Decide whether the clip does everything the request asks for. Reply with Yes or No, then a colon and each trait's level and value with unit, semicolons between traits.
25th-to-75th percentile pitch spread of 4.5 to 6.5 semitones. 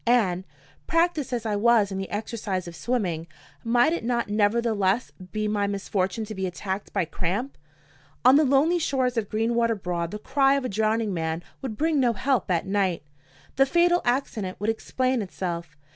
Yes: average, 4.9 semitones